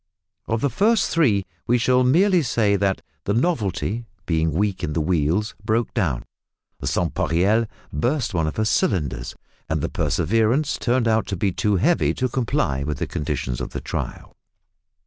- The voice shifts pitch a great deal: Yes, wide, 6.9 semitones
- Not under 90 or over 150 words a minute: No, average, 170 wpm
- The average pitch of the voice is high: No, low, 105 Hz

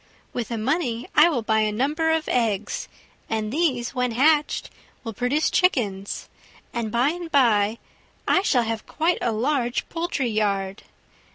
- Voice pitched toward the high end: Yes, high, 245 Hz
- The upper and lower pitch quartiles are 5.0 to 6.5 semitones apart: Yes, wide, 5.5 semitones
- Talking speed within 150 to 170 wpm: Yes, average, 155 wpm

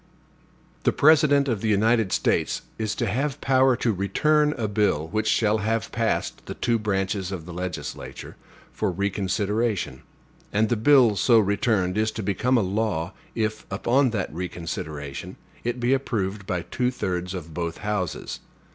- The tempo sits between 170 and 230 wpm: No, average, 155 wpm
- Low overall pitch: Yes, low, 105 Hz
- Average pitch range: Yes, average, 4.2 semitones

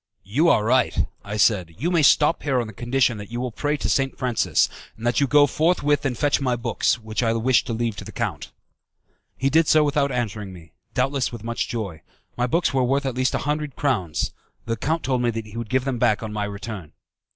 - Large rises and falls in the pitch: No, average, 4.0 semitones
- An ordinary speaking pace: No, fast, 235 wpm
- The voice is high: No, low, 125 Hz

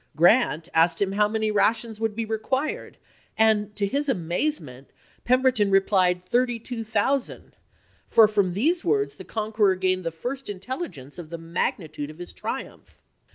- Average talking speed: Yes, average, 155 wpm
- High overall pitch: Yes, high, 210 Hz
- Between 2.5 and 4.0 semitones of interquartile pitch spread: No, average, 5.2 semitones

